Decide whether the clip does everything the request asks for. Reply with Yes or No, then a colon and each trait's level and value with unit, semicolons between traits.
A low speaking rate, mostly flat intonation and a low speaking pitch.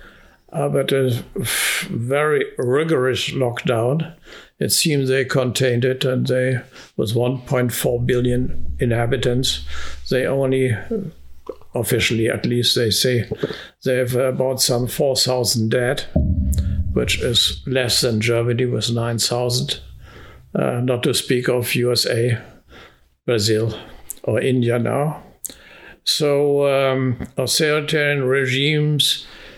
Yes: slow, 105 wpm; narrow, 2.2 semitones; low, 125 Hz